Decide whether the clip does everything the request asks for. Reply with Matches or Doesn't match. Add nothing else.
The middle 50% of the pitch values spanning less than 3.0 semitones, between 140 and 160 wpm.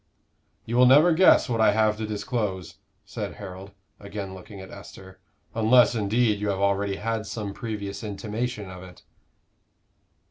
Matches